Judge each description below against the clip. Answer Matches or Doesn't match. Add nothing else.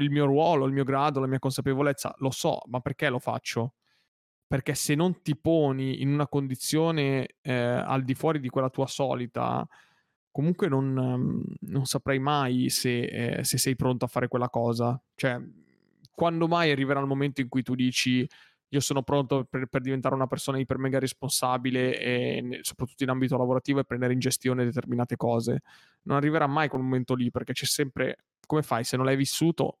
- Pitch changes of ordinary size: Doesn't match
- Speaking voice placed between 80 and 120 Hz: Doesn't match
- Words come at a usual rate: Doesn't match